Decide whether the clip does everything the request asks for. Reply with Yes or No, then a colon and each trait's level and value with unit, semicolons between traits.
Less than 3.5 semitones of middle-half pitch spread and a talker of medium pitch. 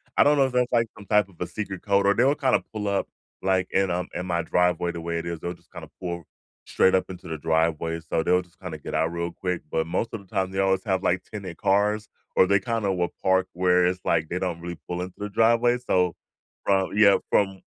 No: average, 2.7 semitones; very low, 95 Hz